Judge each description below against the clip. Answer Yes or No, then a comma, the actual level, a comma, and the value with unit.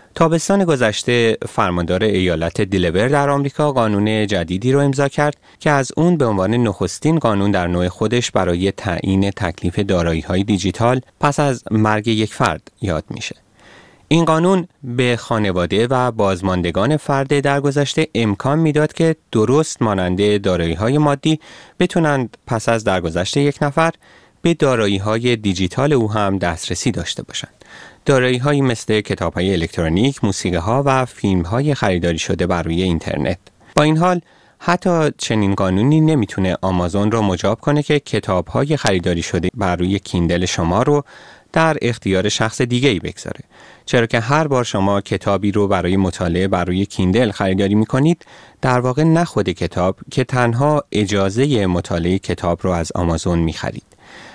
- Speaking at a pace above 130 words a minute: Yes, average, 150 wpm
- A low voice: Yes, low, 110 Hz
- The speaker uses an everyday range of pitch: No, wide, 7.0 semitones